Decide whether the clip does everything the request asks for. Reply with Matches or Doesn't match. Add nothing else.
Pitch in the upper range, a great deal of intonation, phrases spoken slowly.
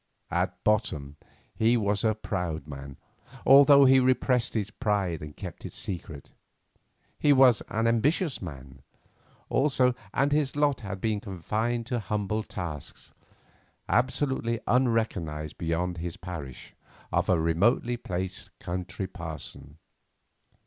Doesn't match